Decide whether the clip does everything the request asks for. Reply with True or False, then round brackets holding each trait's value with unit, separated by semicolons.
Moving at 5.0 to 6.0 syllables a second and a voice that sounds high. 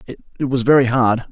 False (5.3 syllables/s; 125 Hz)